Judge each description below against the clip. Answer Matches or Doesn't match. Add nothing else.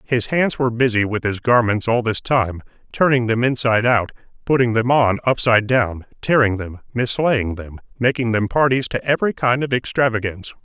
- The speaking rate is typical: Matches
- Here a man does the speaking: Matches